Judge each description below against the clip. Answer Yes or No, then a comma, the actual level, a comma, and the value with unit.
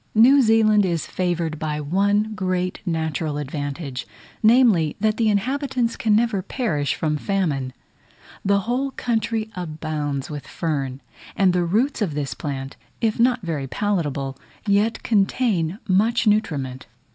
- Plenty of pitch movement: Yes, wide, 6.5 semitones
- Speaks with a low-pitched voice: No, medium, 185 Hz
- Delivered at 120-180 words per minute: Yes, slow, 135 wpm